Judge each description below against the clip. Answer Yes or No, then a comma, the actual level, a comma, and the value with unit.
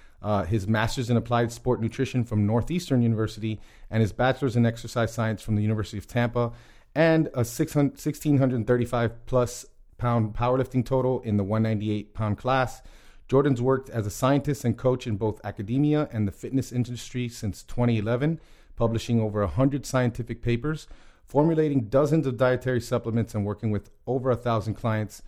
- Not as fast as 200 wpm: Yes, average, 155 wpm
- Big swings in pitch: No, average, 2.9 semitones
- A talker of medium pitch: No, low, 120 Hz